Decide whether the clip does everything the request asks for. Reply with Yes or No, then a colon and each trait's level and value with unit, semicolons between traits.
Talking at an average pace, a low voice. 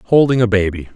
Yes: average, 190 wpm; low, 110 Hz